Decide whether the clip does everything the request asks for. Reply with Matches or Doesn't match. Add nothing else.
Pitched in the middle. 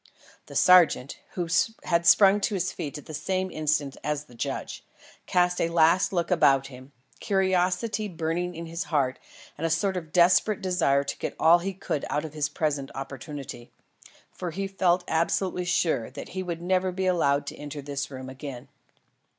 Matches